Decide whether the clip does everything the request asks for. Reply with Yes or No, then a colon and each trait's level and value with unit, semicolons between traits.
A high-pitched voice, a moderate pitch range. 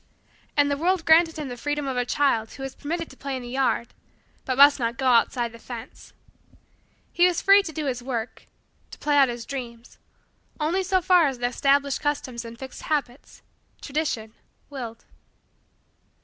Yes: very high, 275 Hz; average, 3.8 semitones